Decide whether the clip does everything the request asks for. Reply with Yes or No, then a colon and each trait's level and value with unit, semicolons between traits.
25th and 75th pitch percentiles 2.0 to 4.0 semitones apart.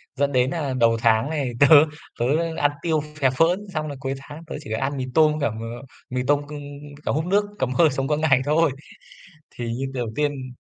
Yes: average, 3.2 semitones